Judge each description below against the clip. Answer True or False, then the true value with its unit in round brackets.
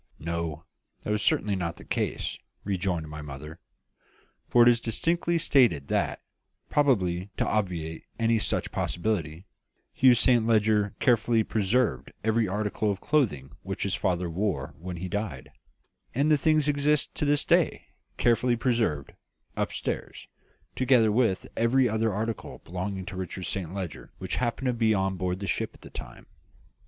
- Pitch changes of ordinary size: True (5.0 semitones)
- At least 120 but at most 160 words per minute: True (155 wpm)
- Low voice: True (105 Hz)